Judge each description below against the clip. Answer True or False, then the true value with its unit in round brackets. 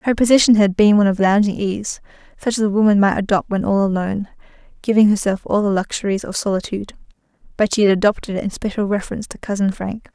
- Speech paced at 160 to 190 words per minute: False (200 wpm)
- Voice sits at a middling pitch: False (205 Hz)